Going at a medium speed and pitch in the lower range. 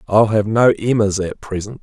Yes: average, 195 wpm; low, 105 Hz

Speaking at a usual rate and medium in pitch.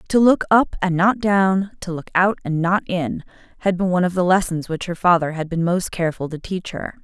No: fast, 240 wpm; medium, 180 Hz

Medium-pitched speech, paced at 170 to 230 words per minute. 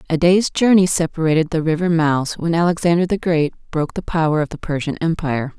Yes: medium, 165 Hz; average, 195 wpm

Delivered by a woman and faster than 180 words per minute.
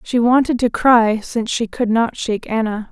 Yes: female; fast, 205 wpm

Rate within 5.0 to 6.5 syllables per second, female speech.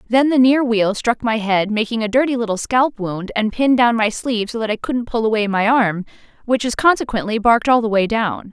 Yes: 5.5 syllables/s; female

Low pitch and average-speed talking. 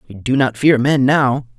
No: low, 130 Hz; fast, 225 wpm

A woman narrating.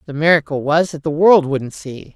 Yes: female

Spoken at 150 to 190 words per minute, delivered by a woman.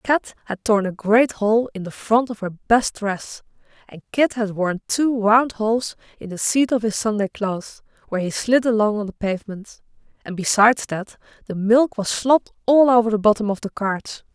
No: average, 200 wpm; female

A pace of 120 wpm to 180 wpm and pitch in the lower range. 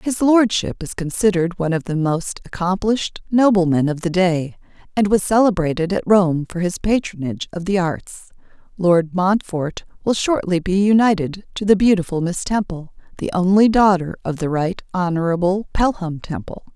No: average, 160 wpm; medium, 185 Hz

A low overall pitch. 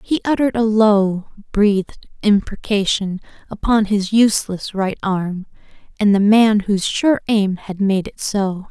No: high, 205 Hz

